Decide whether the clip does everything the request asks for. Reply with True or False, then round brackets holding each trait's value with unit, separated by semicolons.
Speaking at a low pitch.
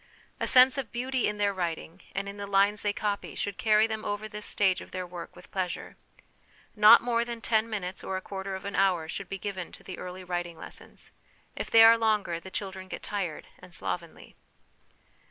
False (200 Hz)